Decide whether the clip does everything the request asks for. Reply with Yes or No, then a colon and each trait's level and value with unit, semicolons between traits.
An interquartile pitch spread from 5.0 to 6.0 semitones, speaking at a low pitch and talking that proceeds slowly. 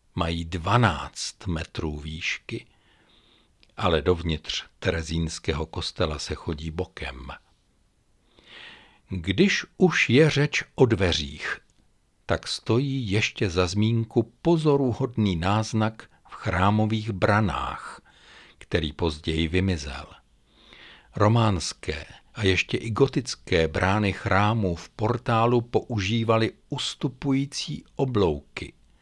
Yes: wide, 5.6 semitones; low, 100 Hz; slow, 85 wpm